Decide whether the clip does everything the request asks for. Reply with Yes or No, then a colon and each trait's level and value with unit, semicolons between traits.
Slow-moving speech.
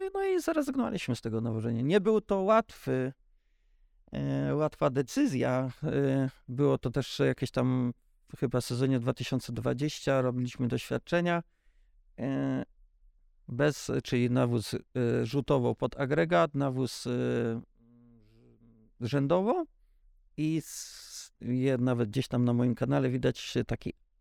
Yes: slow, 100 wpm